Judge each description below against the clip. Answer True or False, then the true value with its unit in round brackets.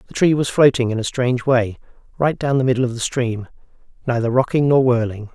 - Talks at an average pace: False (215 wpm)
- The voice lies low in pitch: True (125 Hz)